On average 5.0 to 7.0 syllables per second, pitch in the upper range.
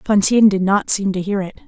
Yes: 5.8 syllables/s; high, 200 Hz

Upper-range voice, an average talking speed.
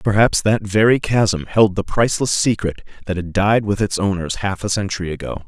No: low, 100 Hz; average, 195 wpm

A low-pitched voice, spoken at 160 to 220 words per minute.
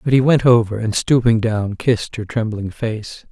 Yes: low, 115 Hz; average, 200 wpm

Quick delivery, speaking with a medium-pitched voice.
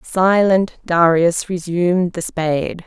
No: slow, 105 wpm; medium, 175 Hz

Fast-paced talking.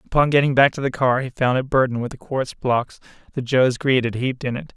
Yes: fast, 265 wpm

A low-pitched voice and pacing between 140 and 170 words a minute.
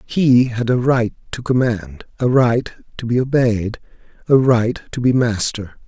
Yes: low, 120 Hz; average, 165 wpm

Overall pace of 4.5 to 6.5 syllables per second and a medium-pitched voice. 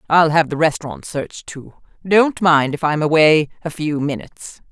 Yes: 5.2 syllables/s; medium, 155 Hz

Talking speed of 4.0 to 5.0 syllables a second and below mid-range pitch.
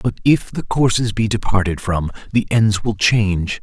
Yes: 4.7 syllables/s; low, 105 Hz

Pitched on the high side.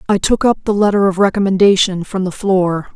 Yes: high, 195 Hz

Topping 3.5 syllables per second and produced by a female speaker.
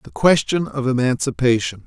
No: 5.1 syllables/s; male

